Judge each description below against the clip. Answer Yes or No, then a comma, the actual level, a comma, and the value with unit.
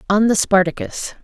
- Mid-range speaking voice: No, high, 200 Hz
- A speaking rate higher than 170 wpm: No, average, 145 wpm